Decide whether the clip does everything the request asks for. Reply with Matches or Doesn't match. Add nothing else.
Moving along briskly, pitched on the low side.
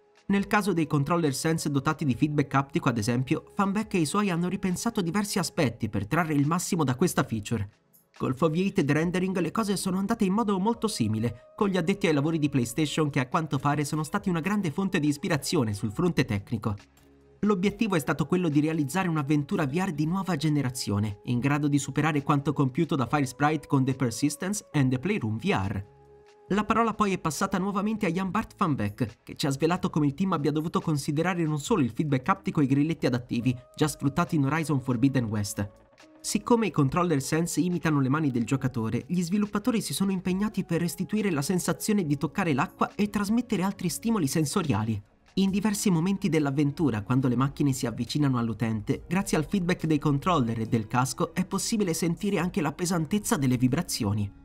Doesn't match